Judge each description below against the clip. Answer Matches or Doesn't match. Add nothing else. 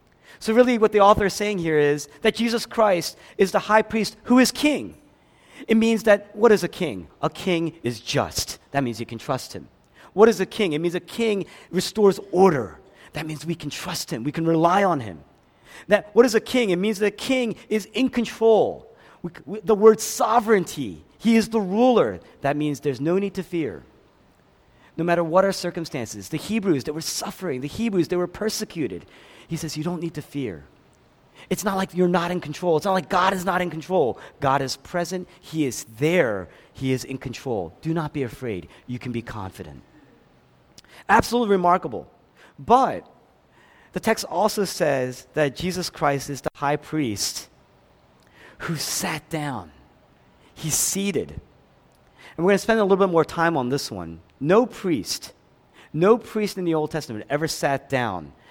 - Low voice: Doesn't match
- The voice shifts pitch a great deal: Matches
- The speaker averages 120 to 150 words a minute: Doesn't match